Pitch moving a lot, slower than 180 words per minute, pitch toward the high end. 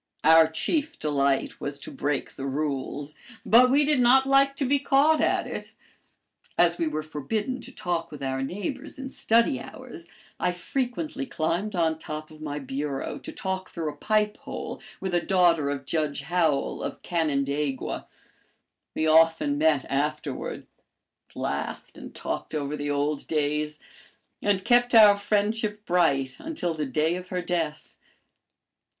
No: wide, 6.4 semitones; average, 155 wpm; medium, 165 Hz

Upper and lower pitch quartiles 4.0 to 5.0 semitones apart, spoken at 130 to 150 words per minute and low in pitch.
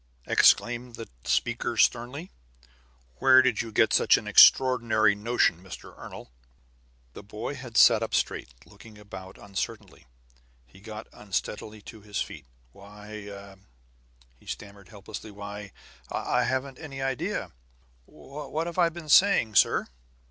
Yes: average, 4.4 semitones; slow, 135 wpm; low, 110 Hz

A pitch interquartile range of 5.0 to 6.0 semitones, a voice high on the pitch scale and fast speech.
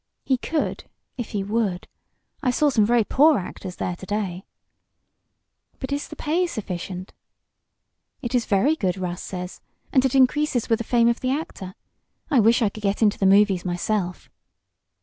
No: wide, 5.4 semitones; high, 220 Hz; average, 170 wpm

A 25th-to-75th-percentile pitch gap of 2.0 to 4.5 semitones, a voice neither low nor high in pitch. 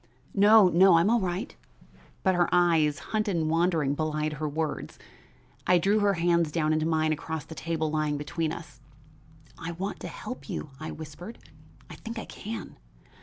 Yes: average, 3.0 semitones; medium, 165 Hz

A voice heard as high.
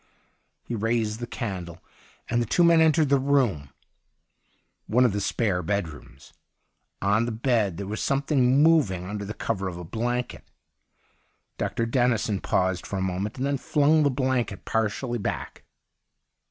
No: low, 115 Hz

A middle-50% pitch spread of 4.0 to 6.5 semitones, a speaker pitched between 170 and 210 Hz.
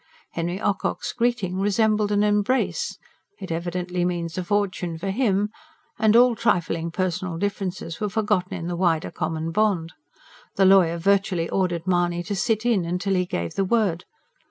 No: average, 3.2 semitones; medium, 185 Hz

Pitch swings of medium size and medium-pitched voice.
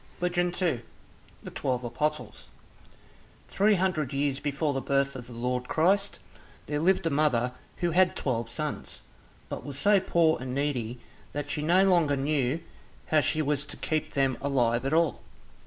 Yes: average, 4.2 semitones; medium, 145 Hz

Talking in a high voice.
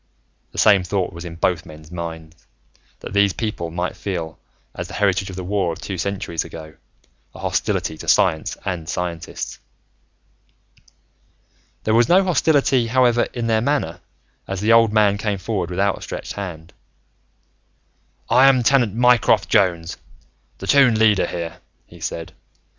No: low, 100 Hz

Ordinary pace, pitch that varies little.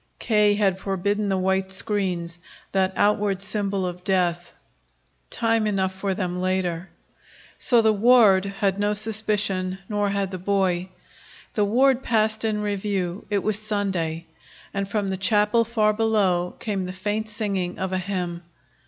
Yes: average, 150 wpm; narrow, 2.1 semitones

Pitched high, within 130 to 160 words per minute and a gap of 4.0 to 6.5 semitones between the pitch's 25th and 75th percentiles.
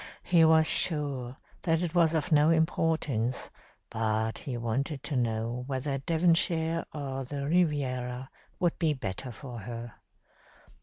No: medium, 140 Hz; average, 140 wpm; average, 4.6 semitones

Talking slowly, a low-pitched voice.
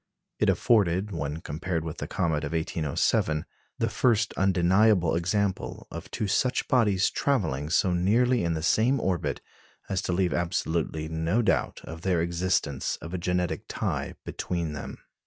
No: average, 155 wpm; very low, 90 Hz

